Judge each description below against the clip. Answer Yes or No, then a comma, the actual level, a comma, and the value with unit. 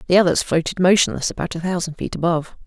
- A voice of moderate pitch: Yes, medium, 175 Hz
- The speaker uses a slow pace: No, fast, 205 wpm